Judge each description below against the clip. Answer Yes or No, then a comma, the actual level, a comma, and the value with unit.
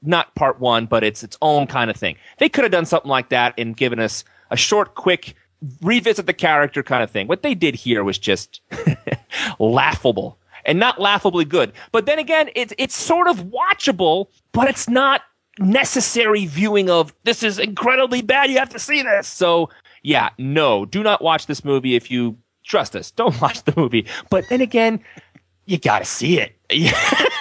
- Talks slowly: No, average, 190 wpm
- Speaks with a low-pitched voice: No, medium, 185 Hz